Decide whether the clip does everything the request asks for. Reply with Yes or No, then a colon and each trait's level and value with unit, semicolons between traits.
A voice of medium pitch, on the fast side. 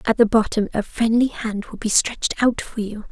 No: high, 220 Hz; fast, 230 wpm